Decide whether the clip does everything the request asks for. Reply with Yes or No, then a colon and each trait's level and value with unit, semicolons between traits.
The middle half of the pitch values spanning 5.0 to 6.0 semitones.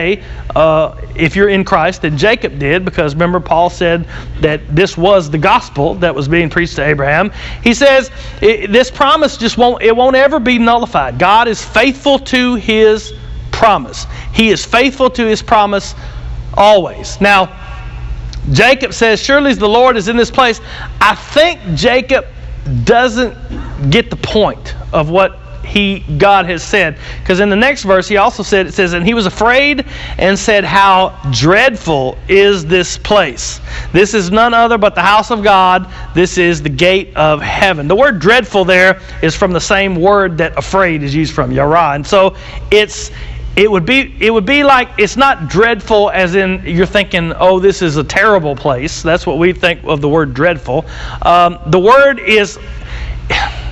Yes: wide, 5.5 semitones